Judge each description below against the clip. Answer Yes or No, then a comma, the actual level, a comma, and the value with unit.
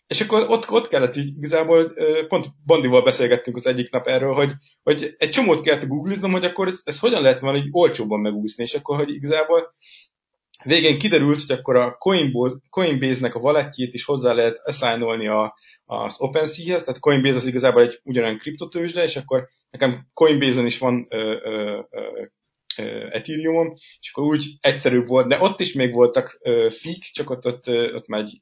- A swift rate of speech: Yes, fast, 170 wpm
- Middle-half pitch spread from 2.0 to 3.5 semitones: No, average, 5.0 semitones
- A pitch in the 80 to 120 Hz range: No, medium, 140 Hz